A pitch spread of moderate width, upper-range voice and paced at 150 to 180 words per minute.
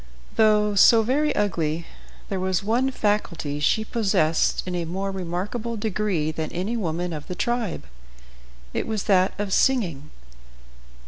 No: average, 4.3 semitones; high, 195 Hz; average, 140 wpm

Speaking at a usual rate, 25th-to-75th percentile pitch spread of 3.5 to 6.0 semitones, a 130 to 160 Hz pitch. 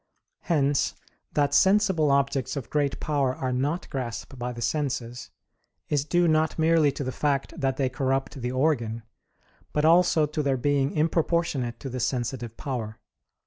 No: average, 155 wpm; average, 3.1 semitones; medium, 140 Hz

